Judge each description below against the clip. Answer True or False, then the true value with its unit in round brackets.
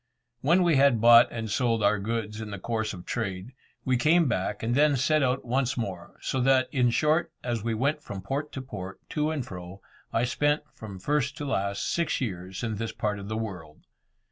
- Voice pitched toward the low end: True (120 Hz)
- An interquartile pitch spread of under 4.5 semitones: False (5.1 semitones)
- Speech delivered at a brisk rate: True (210 wpm)